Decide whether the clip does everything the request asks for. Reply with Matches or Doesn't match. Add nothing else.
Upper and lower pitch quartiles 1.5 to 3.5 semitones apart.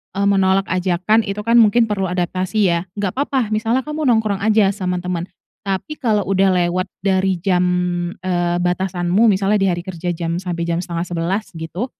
Matches